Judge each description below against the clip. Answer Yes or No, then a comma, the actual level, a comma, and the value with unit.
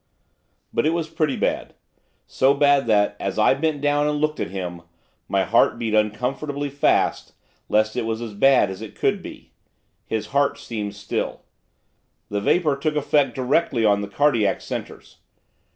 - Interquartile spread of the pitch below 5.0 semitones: No, wide, 5.4 semitones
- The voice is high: No, low, 130 Hz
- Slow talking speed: No, average, 165 wpm